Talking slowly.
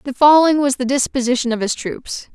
No: fast, 205 wpm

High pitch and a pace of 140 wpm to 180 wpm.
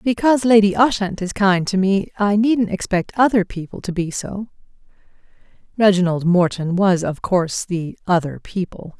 Yes: high, 195 Hz; average, 155 wpm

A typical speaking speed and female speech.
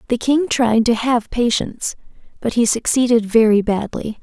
Yes: average, 155 wpm; female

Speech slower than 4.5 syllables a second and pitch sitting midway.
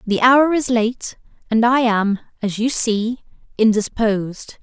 No: 3.8 syllables/s; high, 230 Hz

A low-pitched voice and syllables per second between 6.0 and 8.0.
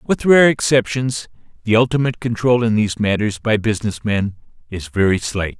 No: low, 110 Hz; 5.4 syllables/s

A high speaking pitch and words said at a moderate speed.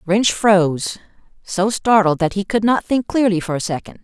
Yes: high, 200 Hz; average, 195 wpm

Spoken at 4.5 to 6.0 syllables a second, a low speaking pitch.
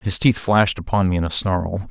Yes: 5.4 syllables/s; very low, 95 Hz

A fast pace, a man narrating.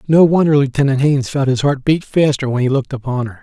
Yes: fast, 245 wpm; male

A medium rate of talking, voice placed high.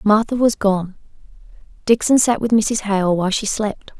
Yes: average, 165 wpm; high, 210 Hz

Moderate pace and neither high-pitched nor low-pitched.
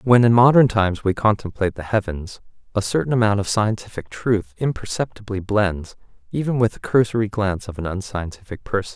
No: average, 165 wpm; low, 105 Hz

